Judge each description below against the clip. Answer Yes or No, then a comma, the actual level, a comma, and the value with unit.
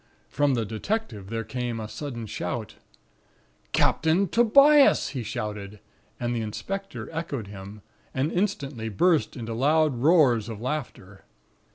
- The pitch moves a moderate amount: No, wide, 6.5 semitones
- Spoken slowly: Yes, slow, 130 wpm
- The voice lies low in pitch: Yes, low, 125 Hz